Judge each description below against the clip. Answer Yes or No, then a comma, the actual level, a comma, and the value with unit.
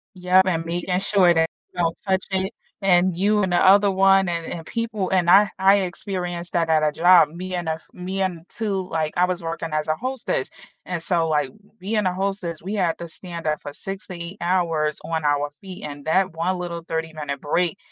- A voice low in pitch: No, medium, 175 Hz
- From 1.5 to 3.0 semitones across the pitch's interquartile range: Yes, average, 2.7 semitones